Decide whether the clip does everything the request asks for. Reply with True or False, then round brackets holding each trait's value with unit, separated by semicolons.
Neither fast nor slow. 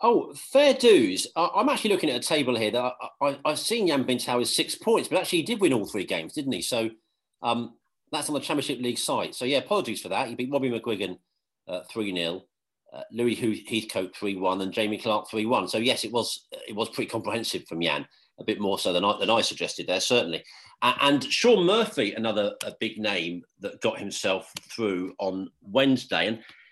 False (215 wpm)